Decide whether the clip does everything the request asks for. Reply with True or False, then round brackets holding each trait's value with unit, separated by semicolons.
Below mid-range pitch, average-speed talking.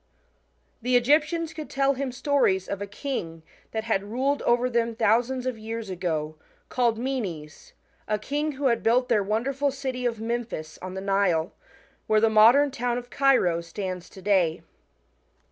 False (230 Hz; 160 wpm)